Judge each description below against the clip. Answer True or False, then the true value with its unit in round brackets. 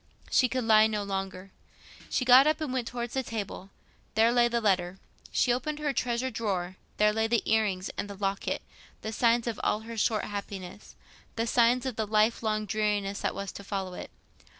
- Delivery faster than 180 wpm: True (190 wpm)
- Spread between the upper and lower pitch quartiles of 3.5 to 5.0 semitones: False (3.0 semitones)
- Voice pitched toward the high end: True (220 Hz)